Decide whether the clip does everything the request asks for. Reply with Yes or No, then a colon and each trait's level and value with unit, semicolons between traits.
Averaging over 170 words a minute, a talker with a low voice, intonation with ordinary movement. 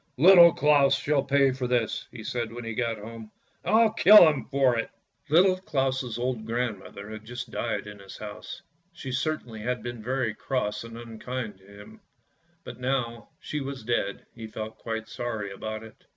Yes: average, 190 wpm; low, 120 Hz; average, 3.6 semitones